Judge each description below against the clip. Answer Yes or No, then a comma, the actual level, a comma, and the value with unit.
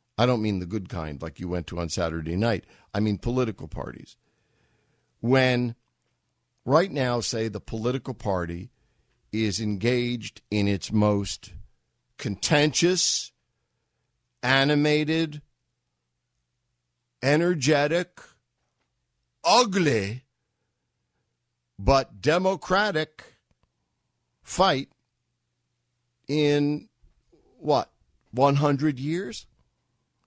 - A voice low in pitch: Yes, low, 120 Hz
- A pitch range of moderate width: No, wide, 8.0 semitones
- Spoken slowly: Yes, slow, 80 wpm